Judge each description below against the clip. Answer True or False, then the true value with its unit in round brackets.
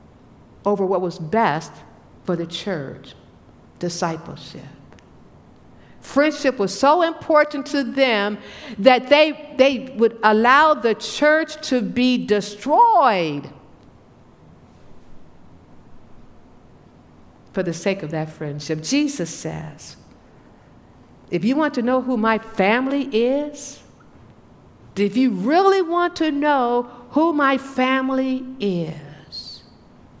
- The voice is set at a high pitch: True (245 Hz)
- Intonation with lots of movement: True (7.0 semitones)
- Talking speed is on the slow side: True (100 wpm)